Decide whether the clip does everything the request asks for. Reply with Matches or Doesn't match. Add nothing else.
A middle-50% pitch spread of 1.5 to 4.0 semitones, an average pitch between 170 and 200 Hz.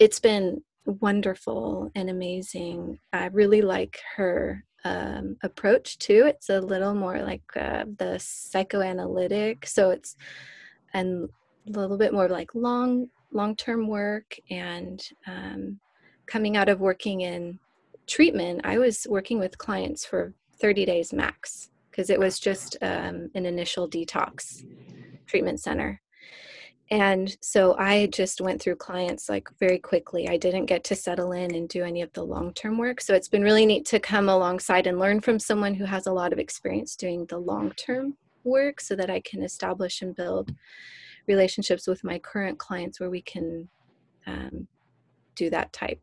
Matches